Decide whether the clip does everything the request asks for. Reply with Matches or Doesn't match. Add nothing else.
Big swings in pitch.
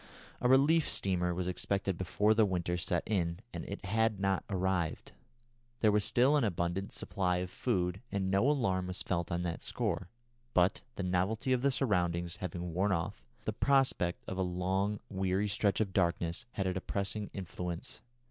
Doesn't match